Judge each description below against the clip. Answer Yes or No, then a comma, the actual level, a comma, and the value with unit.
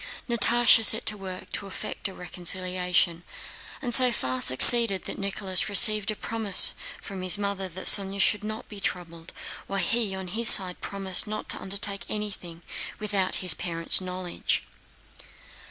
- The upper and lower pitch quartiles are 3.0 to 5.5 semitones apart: No, narrow, 2.6 semitones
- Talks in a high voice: Yes, high, 195 Hz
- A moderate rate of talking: Yes, average, 155 wpm